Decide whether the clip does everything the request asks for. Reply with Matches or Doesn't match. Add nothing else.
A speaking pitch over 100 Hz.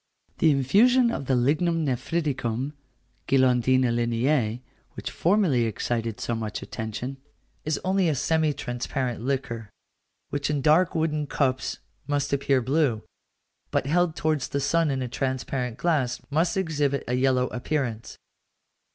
Matches